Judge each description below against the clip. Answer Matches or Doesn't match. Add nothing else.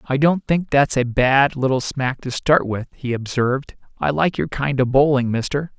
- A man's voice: Matches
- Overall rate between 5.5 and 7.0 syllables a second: Doesn't match